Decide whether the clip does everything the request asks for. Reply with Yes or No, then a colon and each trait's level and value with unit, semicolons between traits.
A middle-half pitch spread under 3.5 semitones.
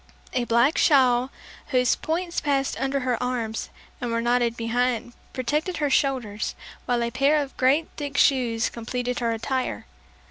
Yes: average, 2.7 semitones